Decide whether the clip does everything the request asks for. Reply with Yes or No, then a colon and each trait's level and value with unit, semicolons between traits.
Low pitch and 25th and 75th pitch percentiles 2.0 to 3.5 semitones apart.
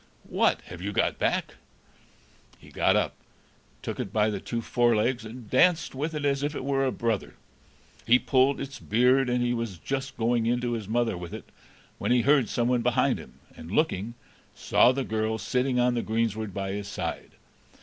Yes: low, 120 Hz; average, 3.1 semitones